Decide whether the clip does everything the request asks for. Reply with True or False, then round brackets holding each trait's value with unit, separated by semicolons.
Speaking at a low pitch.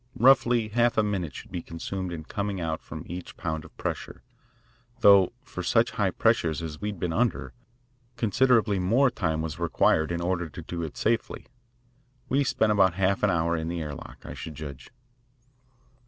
True (90 Hz)